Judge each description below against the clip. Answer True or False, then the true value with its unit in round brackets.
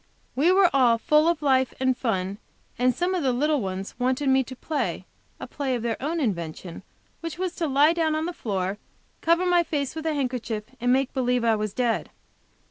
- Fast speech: True (210 wpm)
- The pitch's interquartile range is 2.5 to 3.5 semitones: False (5.2 semitones)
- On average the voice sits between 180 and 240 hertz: False (265 Hz)